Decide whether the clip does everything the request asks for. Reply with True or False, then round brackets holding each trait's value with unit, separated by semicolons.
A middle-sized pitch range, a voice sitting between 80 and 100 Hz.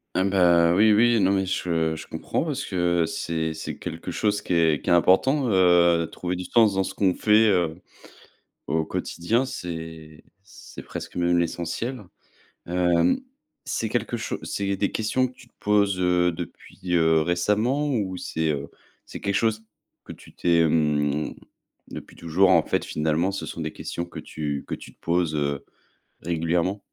True (3.6 semitones; 90 Hz)